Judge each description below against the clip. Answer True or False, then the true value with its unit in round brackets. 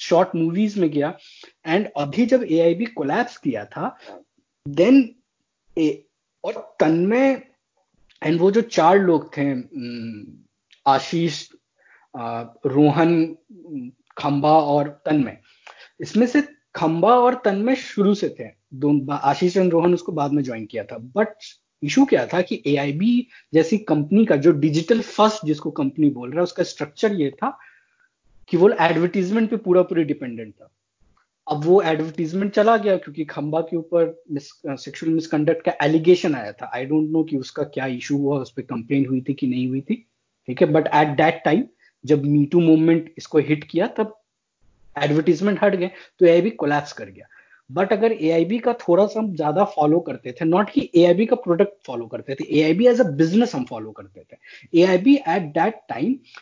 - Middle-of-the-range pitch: True (165 Hz)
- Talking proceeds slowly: False (175 wpm)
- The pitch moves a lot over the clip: True (6.1 semitones)